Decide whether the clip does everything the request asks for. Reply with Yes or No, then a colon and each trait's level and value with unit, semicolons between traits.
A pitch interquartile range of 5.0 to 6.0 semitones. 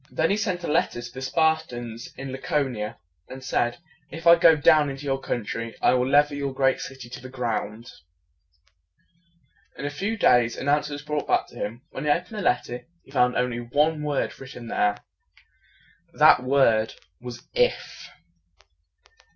No: average, 3.7 semitones